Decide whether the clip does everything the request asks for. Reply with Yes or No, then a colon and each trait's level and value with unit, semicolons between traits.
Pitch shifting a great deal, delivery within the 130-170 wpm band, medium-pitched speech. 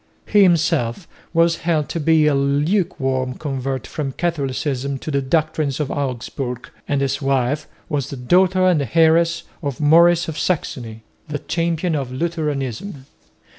No: average, 3.8 semitones; average, 140 wpm; medium, 150 Hz